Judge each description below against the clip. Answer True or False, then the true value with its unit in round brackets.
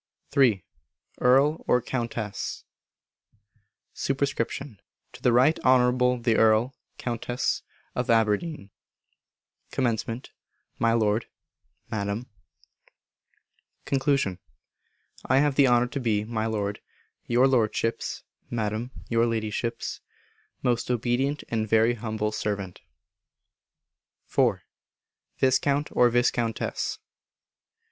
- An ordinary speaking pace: False (90 wpm)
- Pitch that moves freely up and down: False (2.7 semitones)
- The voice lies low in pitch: True (120 Hz)